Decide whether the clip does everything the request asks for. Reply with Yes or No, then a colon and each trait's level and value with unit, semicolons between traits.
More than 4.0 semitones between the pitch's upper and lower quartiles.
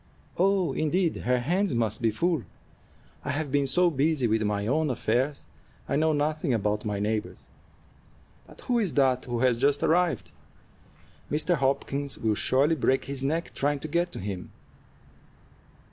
Yes: average, 5.0 semitones